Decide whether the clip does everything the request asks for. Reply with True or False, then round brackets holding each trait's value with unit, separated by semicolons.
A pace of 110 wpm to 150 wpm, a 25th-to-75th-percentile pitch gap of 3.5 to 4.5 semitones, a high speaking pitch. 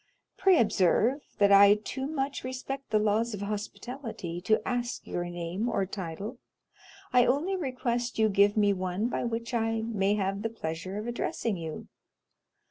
False (165 wpm; 3.8 semitones; 220 Hz)